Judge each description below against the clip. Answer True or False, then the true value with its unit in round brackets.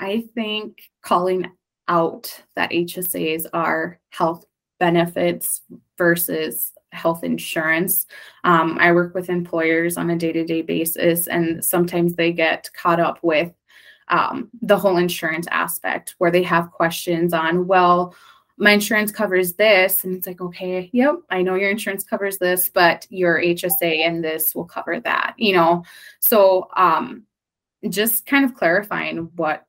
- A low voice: False (175 Hz)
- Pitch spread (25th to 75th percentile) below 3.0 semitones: True (2.5 semitones)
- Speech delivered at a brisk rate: False (150 wpm)